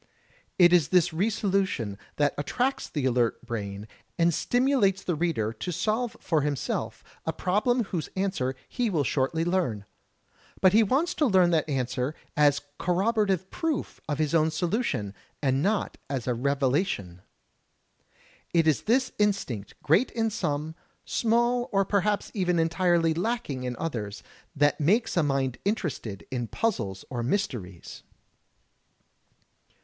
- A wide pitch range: Yes, wide, 7.3 semitones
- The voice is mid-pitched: Yes, medium, 165 Hz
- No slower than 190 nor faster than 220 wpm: No, average, 140 wpm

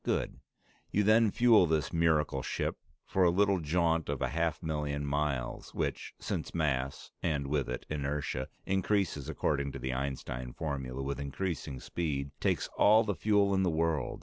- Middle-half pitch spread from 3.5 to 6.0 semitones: Yes, average, 4.5 semitones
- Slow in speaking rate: No, average, 165 wpm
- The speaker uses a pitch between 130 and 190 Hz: No, very low, 75 Hz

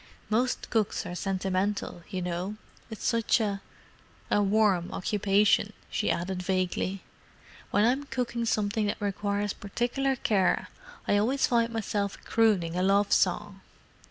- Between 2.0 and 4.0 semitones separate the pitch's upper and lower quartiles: Yes, average, 2.9 semitones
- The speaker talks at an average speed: No, slow, 130 wpm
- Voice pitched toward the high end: Yes, high, 205 Hz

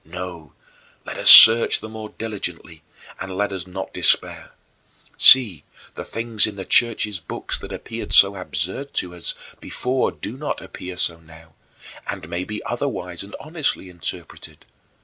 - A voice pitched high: No, very low, 95 Hz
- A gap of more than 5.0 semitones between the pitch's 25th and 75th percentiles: No, average, 4.1 semitones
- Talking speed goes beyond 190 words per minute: No, average, 150 wpm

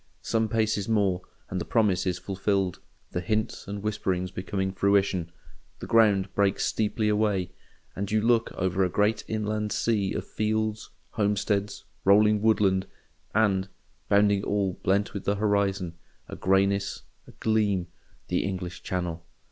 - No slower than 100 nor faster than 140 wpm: Yes, slow, 135 wpm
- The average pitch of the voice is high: No, low, 100 Hz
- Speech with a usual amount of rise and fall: No, narrow, 2.1 semitones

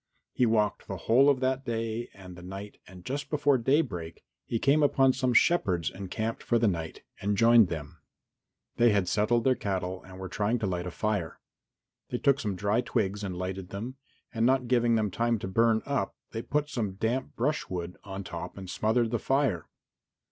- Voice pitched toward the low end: Yes, low, 110 Hz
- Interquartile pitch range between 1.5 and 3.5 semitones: No, average, 4.8 semitones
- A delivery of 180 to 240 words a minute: Yes, average, 190 wpm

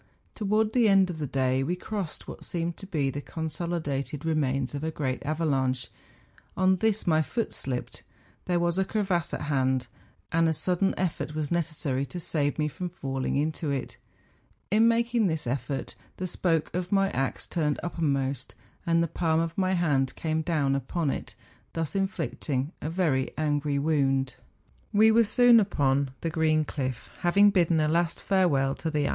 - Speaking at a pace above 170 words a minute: Yes, average, 180 wpm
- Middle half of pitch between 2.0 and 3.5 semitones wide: No, average, 4.4 semitones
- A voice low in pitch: No, medium, 160 Hz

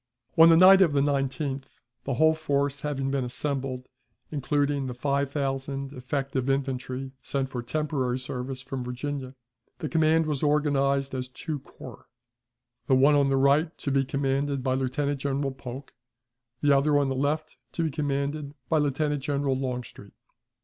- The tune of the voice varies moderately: No, narrow, 1.6 semitones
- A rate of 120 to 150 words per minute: No, average, 160 wpm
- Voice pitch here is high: No, medium, 140 Hz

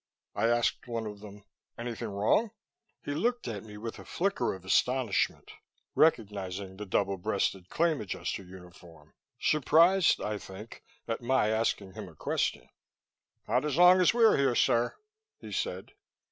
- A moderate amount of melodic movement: No, wide, 6.0 semitones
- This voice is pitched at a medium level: No, low, 110 Hz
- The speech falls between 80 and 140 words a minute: No, average, 150 wpm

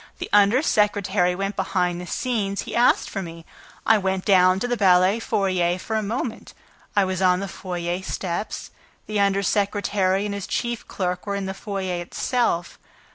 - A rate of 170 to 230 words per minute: Yes, average, 180 wpm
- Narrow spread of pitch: Yes, narrow, 2.2 semitones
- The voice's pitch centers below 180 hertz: No, high, 195 Hz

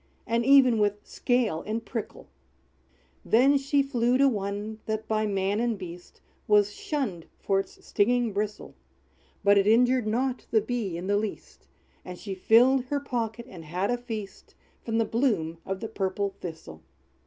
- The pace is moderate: Yes, average, 165 wpm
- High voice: Yes, high, 220 Hz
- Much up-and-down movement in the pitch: No, average, 3.7 semitones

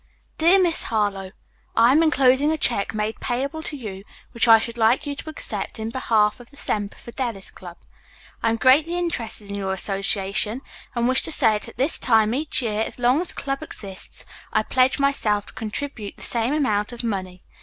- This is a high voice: Yes, high, 235 Hz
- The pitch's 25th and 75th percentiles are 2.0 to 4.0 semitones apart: No, average, 4.7 semitones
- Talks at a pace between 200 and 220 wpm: Yes, fast, 205 wpm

